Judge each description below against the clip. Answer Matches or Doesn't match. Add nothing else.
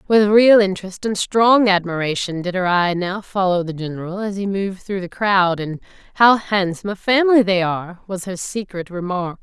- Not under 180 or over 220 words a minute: Matches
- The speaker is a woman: Matches